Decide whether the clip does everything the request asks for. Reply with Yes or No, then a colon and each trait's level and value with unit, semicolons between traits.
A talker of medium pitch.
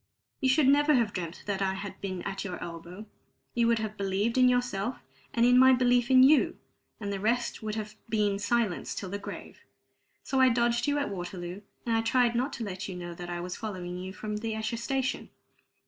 No: high, 215 Hz